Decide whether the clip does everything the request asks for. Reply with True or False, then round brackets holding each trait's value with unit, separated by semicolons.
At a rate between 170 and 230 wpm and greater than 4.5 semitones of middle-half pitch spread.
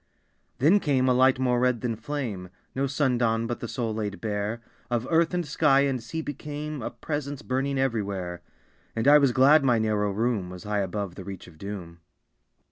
True (195 wpm; 5.0 semitones)